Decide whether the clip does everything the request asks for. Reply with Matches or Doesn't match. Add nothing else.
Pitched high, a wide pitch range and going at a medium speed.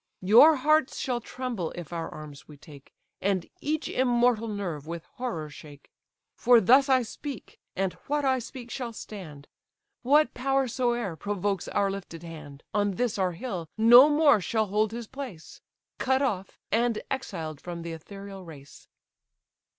Matches